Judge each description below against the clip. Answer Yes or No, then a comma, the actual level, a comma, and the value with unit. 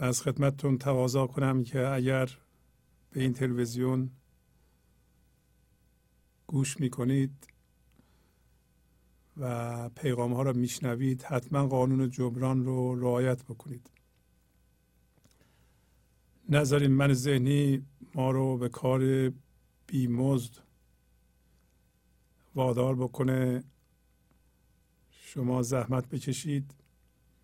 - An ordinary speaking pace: No, slow, 80 wpm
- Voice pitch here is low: Yes, low, 125 Hz